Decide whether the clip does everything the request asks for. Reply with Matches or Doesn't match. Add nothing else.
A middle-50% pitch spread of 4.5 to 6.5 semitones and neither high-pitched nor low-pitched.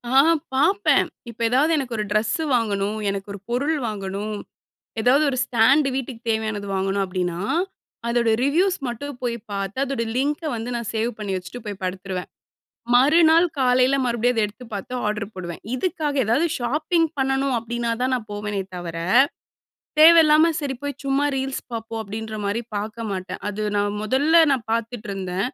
Doesn't match